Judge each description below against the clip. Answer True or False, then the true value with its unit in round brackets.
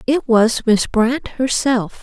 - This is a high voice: True (240 Hz)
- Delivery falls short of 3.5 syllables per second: True (3.2 syllables/s)